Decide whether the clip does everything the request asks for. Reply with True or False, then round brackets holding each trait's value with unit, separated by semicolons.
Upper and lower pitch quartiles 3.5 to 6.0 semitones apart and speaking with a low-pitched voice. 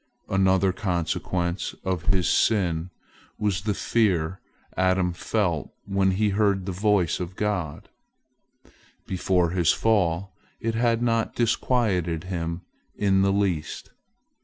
False (2.8 semitones; 95 Hz)